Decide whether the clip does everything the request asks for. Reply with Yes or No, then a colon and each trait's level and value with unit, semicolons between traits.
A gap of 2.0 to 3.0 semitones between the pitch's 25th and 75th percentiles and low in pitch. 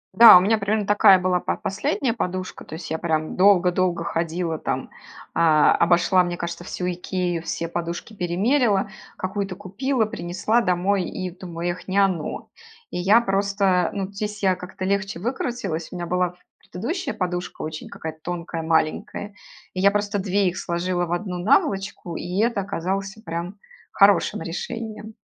No: narrow, 2.6 semitones; medium, 185 Hz